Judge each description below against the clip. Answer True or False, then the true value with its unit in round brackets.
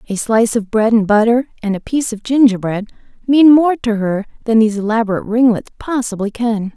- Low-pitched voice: False (225 Hz)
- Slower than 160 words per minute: False (185 wpm)